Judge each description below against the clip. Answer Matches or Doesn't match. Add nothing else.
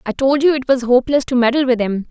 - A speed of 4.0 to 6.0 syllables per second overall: Doesn't match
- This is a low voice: Doesn't match